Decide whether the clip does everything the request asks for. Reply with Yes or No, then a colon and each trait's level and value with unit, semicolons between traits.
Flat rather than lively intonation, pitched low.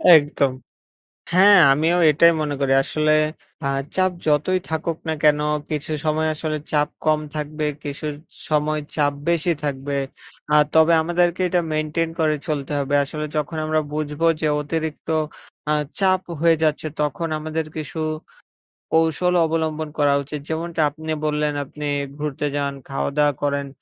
No: narrow, 1.6 semitones; medium, 155 Hz